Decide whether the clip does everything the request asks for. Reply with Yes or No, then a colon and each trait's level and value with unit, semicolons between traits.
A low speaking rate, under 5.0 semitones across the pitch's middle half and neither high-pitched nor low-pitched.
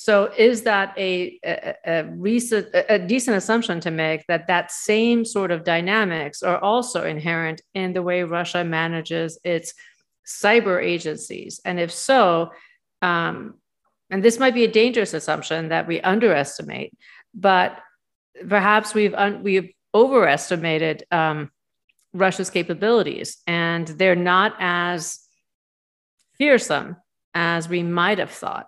Yes: slow, 130 wpm; average, 3.8 semitones; medium, 180 Hz